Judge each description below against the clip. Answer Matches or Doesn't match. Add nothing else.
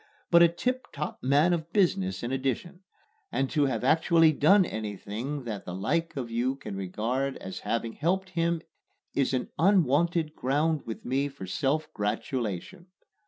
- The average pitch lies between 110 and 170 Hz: Matches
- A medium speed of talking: Matches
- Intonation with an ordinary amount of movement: Doesn't match